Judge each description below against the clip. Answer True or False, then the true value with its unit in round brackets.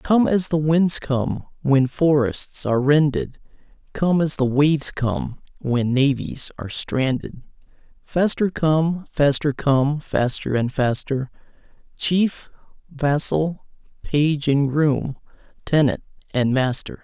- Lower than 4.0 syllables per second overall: True (3.5 syllables/s)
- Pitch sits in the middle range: True (145 Hz)